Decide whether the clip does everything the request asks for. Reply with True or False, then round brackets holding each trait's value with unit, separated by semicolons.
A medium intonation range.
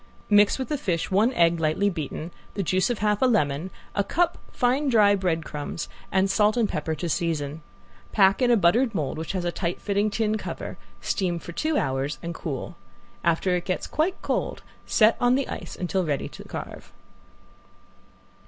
True (4.7 semitones)